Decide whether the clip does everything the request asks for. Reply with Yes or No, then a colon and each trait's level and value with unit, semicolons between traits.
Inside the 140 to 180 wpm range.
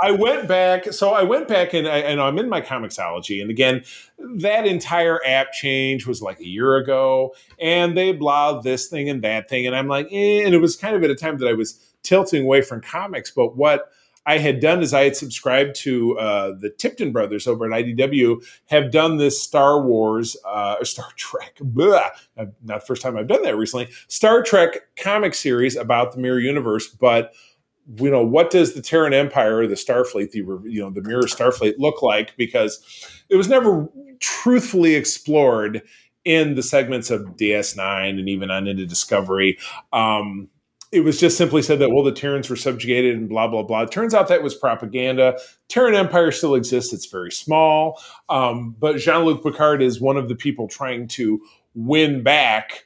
No: average, 195 wpm